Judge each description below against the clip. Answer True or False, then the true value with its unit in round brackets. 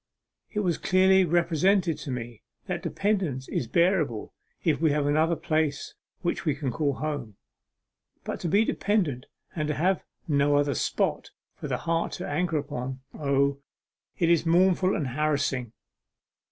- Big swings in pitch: False (3.8 semitones)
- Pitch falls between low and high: True (155 Hz)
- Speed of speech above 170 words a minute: False (155 wpm)